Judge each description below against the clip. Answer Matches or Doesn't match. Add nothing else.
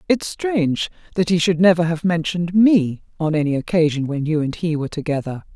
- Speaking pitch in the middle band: Matches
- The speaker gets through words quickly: Doesn't match